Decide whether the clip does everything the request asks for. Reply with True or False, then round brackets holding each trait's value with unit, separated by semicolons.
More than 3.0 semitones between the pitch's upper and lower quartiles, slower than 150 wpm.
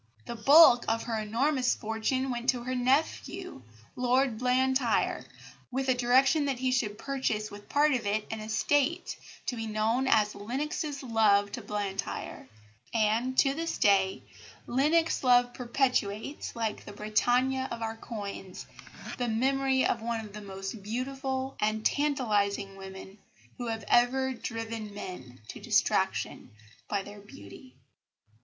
True (3.8 semitones; 140 wpm)